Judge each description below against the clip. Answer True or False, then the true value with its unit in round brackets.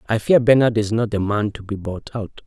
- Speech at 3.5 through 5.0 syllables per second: False (5.4 syllables/s)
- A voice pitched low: True (110 Hz)